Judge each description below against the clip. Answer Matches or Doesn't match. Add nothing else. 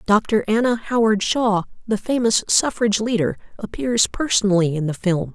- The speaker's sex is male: Doesn't match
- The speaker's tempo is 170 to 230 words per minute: Doesn't match